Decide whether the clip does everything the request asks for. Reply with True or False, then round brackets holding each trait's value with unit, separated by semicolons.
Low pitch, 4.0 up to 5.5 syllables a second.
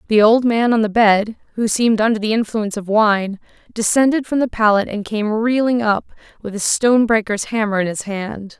False (220 Hz; 5.3 syllables/s)